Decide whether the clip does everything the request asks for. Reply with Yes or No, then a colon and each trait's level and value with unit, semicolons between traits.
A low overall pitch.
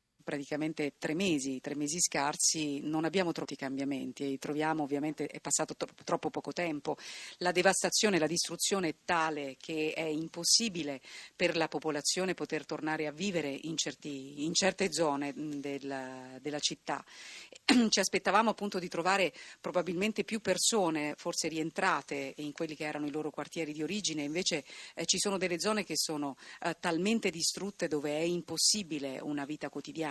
No: medium, 155 Hz